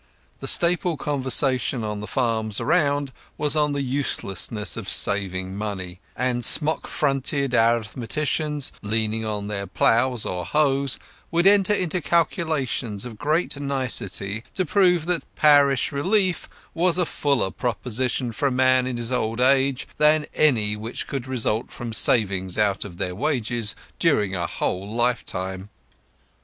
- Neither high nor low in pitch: No, low, 125 Hz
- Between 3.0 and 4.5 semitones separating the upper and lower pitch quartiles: No, wide, 5.6 semitones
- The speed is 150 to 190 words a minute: No, average, 140 wpm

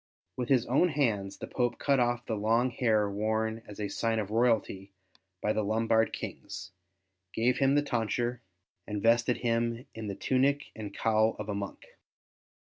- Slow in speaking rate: No, average, 170 wpm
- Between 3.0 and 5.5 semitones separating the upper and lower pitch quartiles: No, narrow, 2.4 semitones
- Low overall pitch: Yes, low, 115 Hz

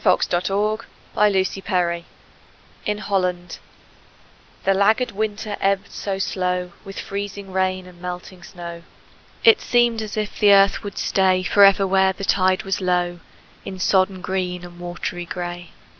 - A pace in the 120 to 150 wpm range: Yes, average, 145 wpm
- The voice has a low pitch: No, high, 190 Hz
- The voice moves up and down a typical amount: No, narrow, 2.0 semitones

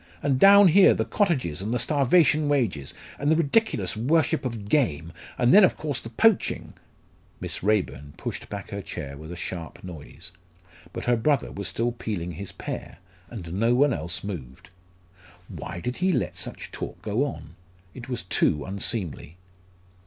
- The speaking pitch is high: No, low, 115 Hz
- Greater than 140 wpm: Yes, average, 170 wpm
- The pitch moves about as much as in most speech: No, wide, 8.5 semitones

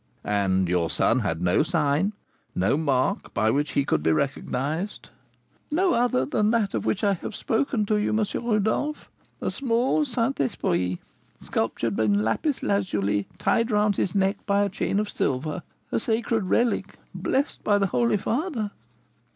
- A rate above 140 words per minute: Yes, average, 160 wpm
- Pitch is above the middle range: Yes, high, 195 Hz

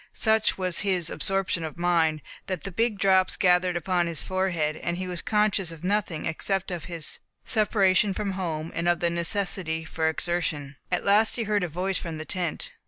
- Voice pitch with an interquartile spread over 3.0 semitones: No, average, 2.7 semitones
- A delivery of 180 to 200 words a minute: Yes, average, 190 wpm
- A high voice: No, medium, 180 Hz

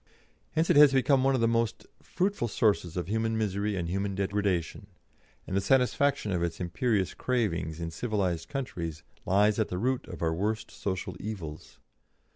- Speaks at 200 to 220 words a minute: No, average, 170 wpm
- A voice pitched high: No, low, 105 Hz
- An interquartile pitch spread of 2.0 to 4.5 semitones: No, average, 5.1 semitones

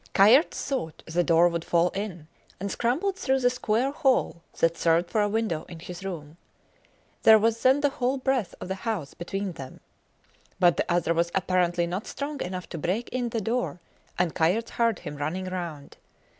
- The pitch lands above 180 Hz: Yes, high, 190 Hz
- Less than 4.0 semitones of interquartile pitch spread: No, wide, 5.5 semitones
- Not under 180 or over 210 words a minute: Yes, average, 185 wpm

